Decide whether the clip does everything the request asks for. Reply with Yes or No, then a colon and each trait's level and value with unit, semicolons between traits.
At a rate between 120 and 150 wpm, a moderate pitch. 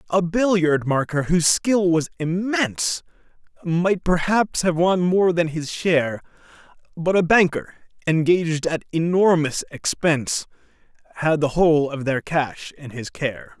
Yes: slow, 135 wpm; medium, 165 Hz